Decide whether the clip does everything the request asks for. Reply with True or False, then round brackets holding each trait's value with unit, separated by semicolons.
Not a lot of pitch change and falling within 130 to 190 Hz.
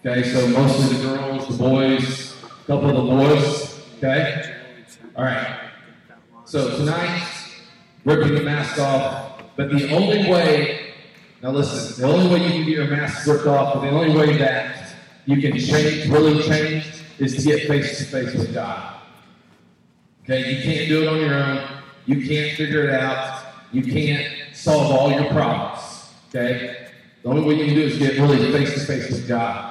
True (2.3 semitones; 140 Hz)